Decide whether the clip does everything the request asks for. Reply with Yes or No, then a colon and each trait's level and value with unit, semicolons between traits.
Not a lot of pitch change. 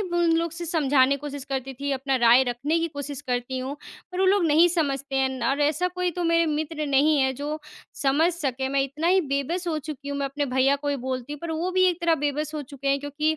No: average, 3.4 semitones